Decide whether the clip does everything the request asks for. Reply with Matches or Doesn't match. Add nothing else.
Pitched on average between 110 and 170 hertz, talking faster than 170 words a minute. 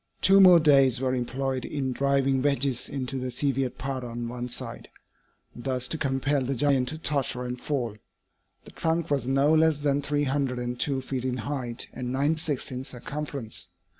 Matches